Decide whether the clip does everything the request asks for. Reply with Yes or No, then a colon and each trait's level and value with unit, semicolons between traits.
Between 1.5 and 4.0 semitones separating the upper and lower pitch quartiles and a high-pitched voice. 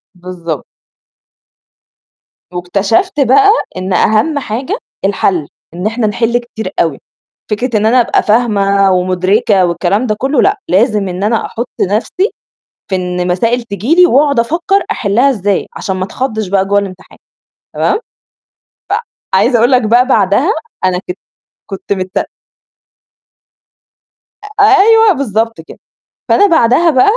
No: wide, 5.5 semitones; high, 215 Hz